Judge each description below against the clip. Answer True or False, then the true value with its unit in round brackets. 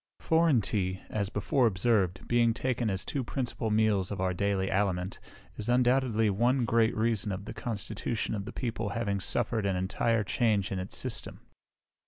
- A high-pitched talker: False (110 Hz)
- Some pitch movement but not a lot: True (3.3 semitones)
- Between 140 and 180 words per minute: True (170 wpm)